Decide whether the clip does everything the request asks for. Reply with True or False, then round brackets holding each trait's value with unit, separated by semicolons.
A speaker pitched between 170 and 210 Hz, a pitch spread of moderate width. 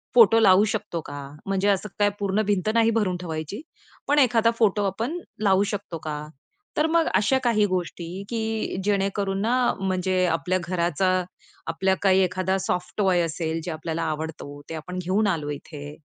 True (190 Hz; 3.7 semitones)